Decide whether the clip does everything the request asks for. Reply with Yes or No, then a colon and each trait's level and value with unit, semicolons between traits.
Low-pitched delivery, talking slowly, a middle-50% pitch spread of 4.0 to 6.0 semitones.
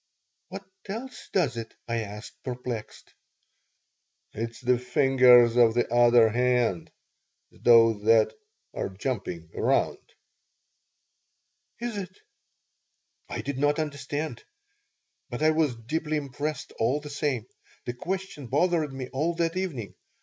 Yes: low, 130 Hz; slow, 120 wpm; average, 4.8 semitones